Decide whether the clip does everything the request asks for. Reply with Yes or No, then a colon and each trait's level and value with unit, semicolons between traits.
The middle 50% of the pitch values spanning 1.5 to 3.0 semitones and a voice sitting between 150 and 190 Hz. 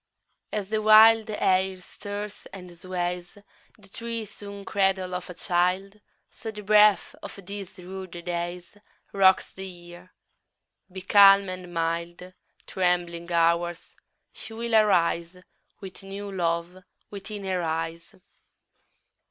Yes: narrow, 2.6 semitones; medium, 185 Hz